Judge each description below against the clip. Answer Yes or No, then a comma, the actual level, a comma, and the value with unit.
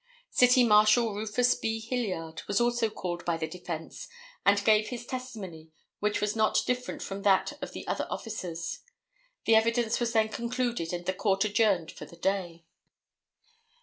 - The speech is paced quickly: No, average, 160 wpm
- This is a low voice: No, high, 210 Hz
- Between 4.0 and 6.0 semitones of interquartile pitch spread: Yes, average, 4.3 semitones